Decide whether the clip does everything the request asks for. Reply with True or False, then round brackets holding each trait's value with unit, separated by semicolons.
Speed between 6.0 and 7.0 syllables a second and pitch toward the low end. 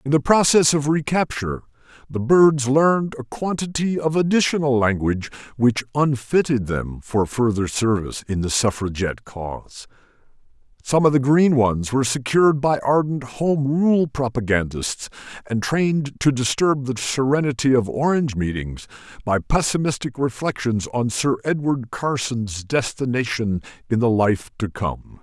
False (4.7 syllables/s; 130 Hz)